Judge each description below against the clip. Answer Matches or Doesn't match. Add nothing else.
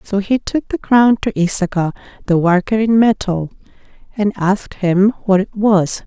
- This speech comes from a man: Doesn't match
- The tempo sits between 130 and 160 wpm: Doesn't match